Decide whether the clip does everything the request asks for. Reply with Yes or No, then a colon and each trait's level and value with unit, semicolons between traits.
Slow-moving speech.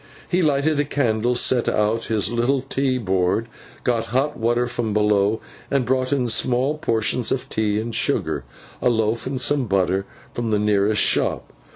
No: average, 170 wpm